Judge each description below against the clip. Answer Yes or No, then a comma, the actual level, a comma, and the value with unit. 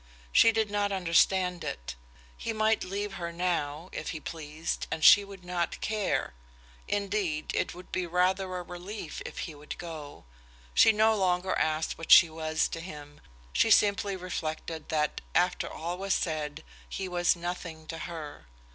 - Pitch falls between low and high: Yes, medium, 175 Hz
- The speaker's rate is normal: Yes, average, 165 wpm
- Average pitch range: Yes, average, 3.5 semitones